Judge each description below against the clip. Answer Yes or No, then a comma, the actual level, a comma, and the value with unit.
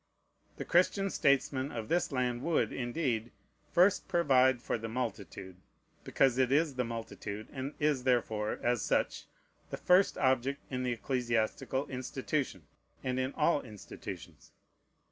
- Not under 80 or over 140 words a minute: Yes, slow, 135 wpm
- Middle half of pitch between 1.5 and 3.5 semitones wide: Yes, average, 3.0 semitones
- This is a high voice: No, low, 130 Hz